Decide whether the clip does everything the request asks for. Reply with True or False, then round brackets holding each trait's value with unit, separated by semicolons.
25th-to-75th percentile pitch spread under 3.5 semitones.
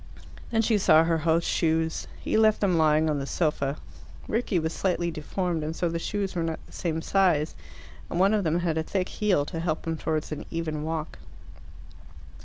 True (2.7 semitones)